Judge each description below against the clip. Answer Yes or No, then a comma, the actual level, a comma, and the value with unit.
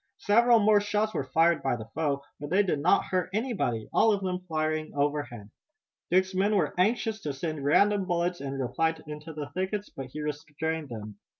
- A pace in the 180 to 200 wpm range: Yes, average, 190 wpm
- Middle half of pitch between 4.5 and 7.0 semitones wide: Yes, wide, 5.4 semitones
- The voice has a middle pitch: Yes, medium, 160 Hz